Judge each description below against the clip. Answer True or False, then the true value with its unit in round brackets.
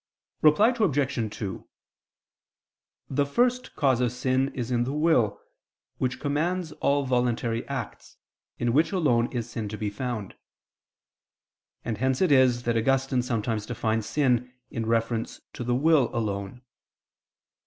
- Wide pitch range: False (3.6 semitones)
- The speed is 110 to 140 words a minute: True (135 wpm)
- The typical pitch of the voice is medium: False (125 Hz)